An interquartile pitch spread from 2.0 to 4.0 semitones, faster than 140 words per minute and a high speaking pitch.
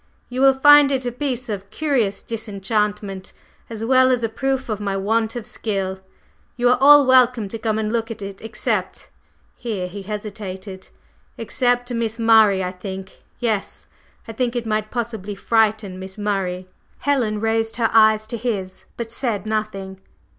Yes: average, 3.3 semitones; average, 170 wpm; high, 220 Hz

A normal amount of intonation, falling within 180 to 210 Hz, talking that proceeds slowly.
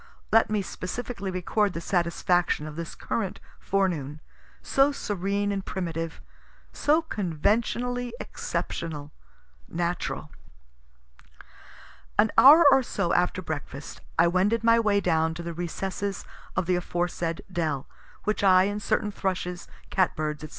Yes: average, 3.7 semitones; medium, 185 Hz; slow, 130 wpm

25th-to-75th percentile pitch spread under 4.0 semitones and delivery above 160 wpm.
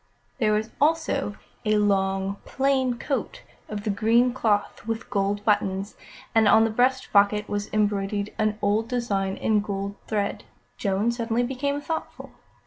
No: average, 2.8 semitones; average, 145 wpm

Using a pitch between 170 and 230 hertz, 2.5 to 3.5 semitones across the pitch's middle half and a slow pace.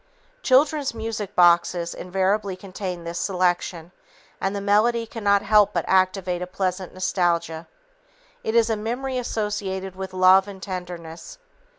Yes: high, 190 Hz; average, 2.8 semitones; slow, 130 wpm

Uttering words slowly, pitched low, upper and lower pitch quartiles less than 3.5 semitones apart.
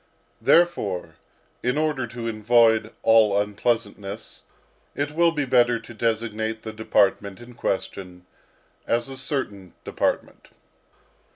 Yes: slow, 110 wpm; low, 115 Hz; average, 3.1 semitones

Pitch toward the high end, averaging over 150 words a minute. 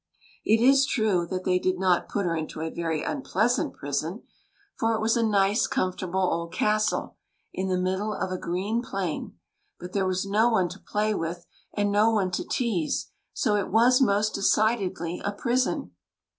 Yes: high, 195 Hz; average, 185 wpm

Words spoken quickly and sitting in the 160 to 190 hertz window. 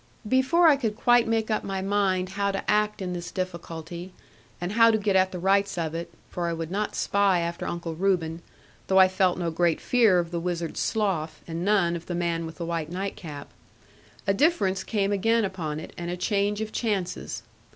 Yes: fast, 210 wpm; medium, 185 Hz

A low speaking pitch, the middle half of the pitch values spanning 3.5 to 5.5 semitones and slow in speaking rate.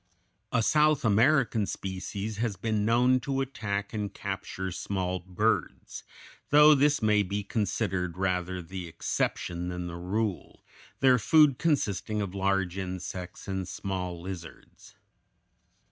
Yes: low, 100 Hz; average, 3.9 semitones; slow, 125 wpm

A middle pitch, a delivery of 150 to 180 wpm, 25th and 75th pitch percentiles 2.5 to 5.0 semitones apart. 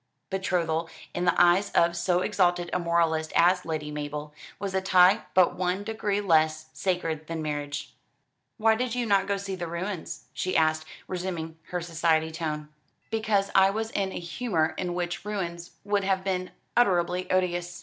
Yes: medium, 175 Hz; average, 170 wpm; average, 2.9 semitones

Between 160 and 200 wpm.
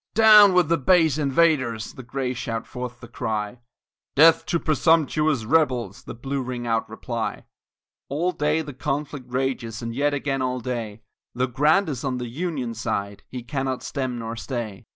Yes: average, 170 wpm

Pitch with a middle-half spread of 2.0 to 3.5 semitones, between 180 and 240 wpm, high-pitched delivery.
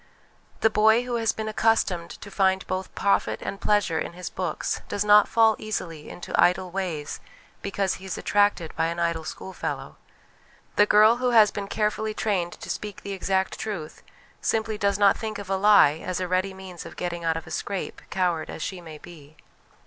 Yes: average, 3.2 semitones; average, 195 wpm; high, 195 Hz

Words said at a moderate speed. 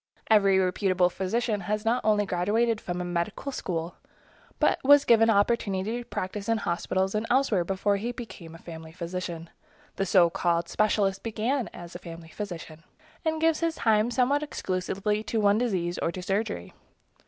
Yes: average, 165 wpm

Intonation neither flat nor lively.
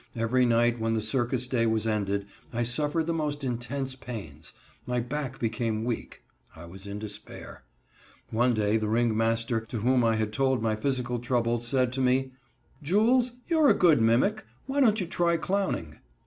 Yes: average, 3.4 semitones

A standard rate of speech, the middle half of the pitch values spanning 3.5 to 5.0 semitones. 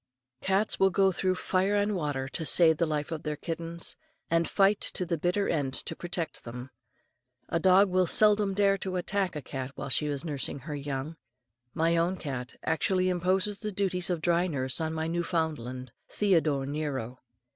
Yes: average, 180 wpm; average, 4.1 semitones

